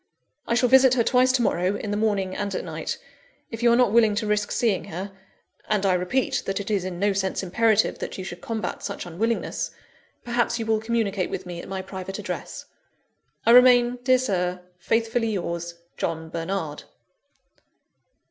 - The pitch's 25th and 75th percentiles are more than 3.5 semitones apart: Yes, average, 4.0 semitones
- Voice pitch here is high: Yes, high, 205 Hz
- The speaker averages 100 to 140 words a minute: No, average, 185 wpm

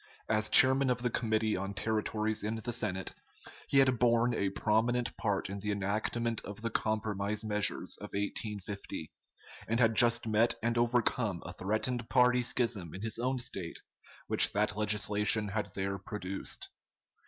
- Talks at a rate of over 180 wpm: No, average, 155 wpm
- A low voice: Yes, low, 110 Hz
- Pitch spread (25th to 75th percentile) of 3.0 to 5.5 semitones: No, narrow, 2.6 semitones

